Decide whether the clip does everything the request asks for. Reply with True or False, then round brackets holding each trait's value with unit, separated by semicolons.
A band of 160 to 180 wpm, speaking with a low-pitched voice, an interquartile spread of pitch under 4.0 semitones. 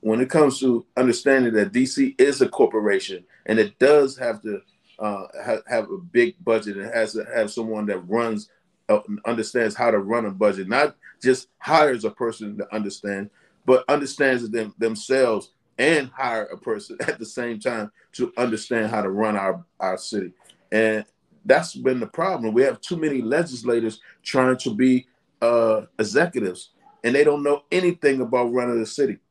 False (175 wpm; 120 Hz; 4.3 semitones)